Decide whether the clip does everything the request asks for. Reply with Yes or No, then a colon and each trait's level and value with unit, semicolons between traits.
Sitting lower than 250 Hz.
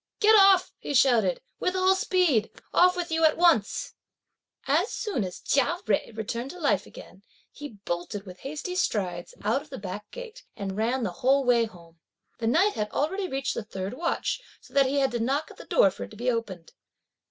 No: very high, 265 Hz